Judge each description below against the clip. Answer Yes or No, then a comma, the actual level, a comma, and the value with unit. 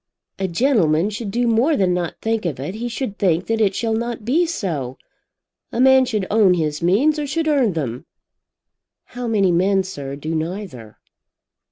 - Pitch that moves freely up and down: Yes, wide, 6.0 semitones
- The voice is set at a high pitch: Yes, high, 200 Hz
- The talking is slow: No, average, 180 wpm